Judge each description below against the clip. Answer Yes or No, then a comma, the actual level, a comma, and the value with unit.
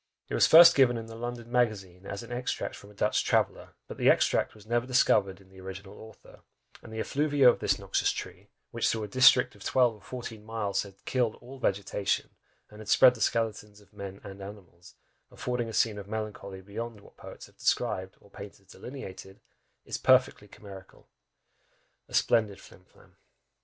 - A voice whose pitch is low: Yes, low, 110 Hz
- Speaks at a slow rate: No, average, 190 wpm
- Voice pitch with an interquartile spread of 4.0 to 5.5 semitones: No, average, 3.4 semitones